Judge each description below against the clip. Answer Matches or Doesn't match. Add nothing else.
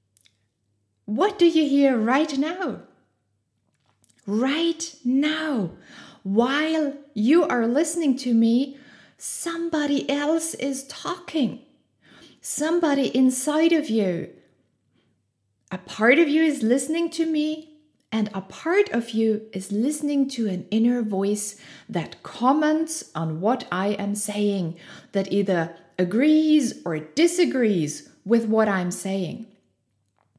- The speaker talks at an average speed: Doesn't match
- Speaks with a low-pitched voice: Doesn't match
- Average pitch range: Doesn't match